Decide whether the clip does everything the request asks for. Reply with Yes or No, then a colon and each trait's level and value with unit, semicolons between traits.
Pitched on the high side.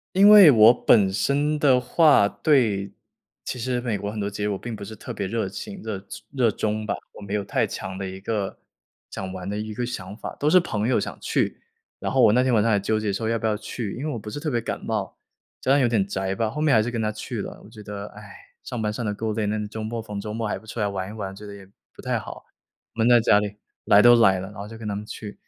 No: low, 110 Hz